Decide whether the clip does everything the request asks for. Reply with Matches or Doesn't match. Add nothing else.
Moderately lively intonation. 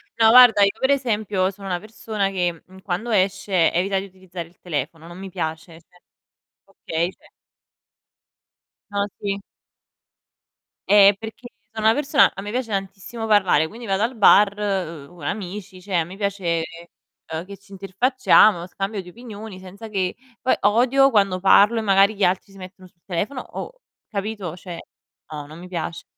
Matches